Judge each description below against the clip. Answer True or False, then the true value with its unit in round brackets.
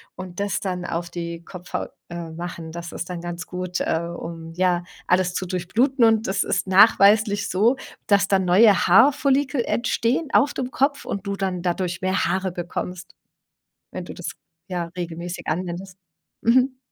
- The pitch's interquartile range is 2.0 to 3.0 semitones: False (3.5 semitones)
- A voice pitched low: False (185 Hz)